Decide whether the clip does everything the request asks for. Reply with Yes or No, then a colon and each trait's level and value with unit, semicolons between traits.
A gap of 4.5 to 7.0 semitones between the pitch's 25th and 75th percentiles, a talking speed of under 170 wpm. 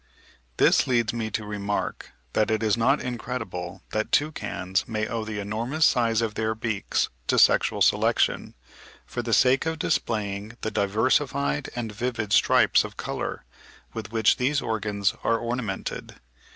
No: average, 2.7 semitones; average, 150 wpm